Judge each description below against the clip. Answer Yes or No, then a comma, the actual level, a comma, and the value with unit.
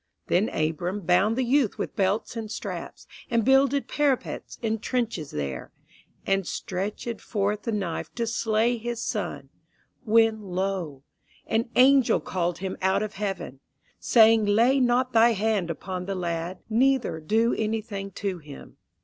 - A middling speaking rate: Yes, average, 145 wpm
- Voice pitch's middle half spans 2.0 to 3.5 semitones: No, average, 3.9 semitones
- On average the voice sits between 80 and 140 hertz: No, high, 215 Hz